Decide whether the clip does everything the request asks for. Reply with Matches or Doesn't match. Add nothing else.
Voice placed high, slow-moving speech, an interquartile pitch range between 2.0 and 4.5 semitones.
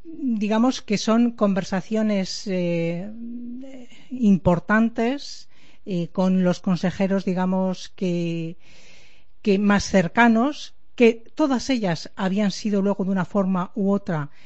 Matches